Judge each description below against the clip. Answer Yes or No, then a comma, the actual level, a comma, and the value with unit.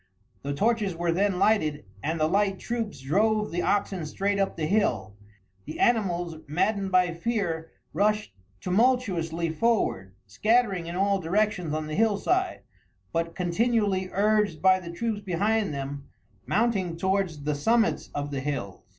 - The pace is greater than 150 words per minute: No, average, 145 wpm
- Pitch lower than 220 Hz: Yes, high, 190 Hz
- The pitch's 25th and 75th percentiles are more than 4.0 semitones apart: Yes, average, 4.6 semitones